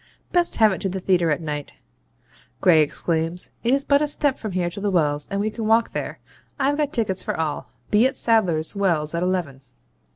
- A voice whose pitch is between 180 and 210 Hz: Yes, high, 190 Hz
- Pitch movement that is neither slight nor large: No, wide, 5.7 semitones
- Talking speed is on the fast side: Yes, fast, 215 wpm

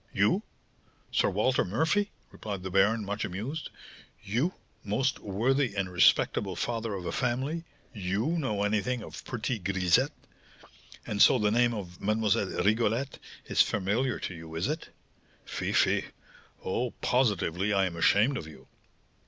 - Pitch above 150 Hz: No, low, 105 Hz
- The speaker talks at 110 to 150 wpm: Yes, average, 145 wpm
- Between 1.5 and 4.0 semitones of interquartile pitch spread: No, average, 4.4 semitones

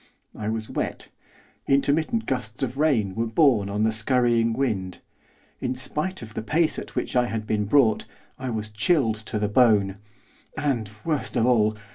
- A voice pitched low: Yes, low, 115 Hz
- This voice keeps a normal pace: Yes, average, 170 wpm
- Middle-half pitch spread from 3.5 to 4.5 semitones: Yes, average, 4.0 semitones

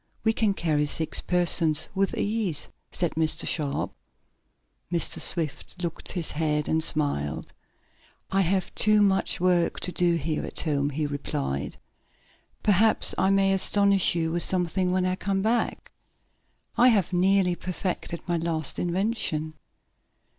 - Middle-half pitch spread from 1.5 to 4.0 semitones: Yes, average, 3.6 semitones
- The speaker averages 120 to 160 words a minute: Yes, average, 140 wpm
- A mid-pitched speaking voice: Yes, medium, 175 Hz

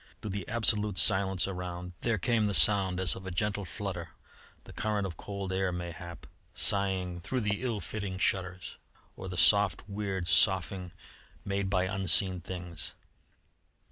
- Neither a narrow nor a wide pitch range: No, narrow, 2.1 semitones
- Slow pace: No, average, 150 wpm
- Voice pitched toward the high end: No, very low, 95 Hz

